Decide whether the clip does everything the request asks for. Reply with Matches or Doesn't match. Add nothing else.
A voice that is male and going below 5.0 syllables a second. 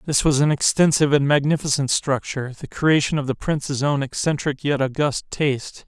Doesn't match